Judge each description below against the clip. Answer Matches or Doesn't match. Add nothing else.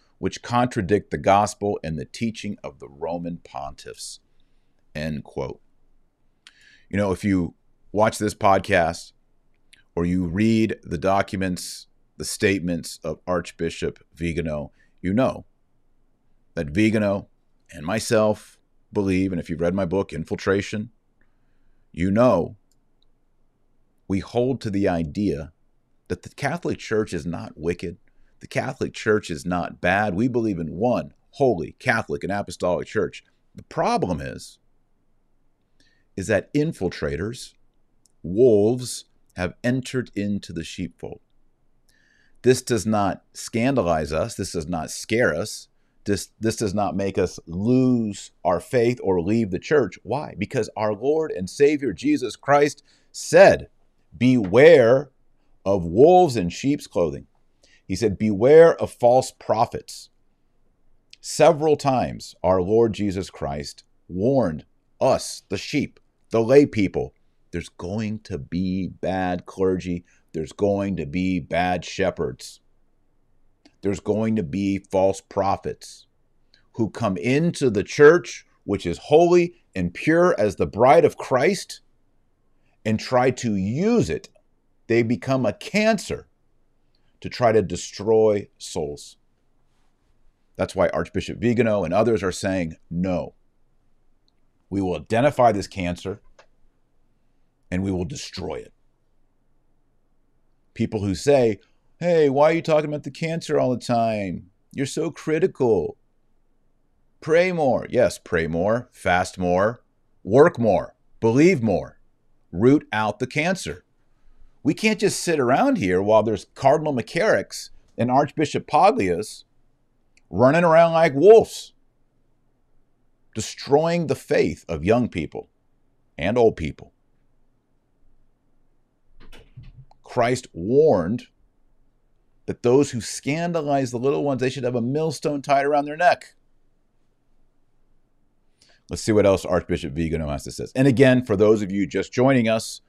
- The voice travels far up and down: Matches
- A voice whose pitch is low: Matches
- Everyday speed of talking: Doesn't match